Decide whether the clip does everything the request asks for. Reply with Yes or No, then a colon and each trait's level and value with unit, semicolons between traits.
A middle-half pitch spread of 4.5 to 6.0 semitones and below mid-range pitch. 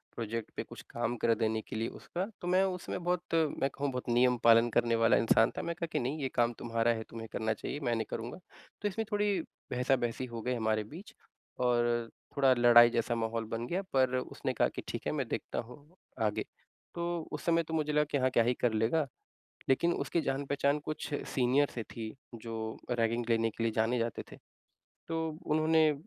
Yes: average, 4.8 semitones; low, 125 Hz